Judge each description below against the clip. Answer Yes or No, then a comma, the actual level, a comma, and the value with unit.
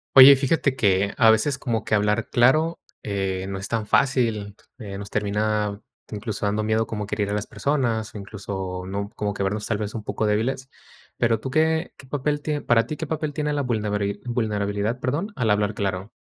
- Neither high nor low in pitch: No, low, 110 Hz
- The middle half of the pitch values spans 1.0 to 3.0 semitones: No, average, 4.3 semitones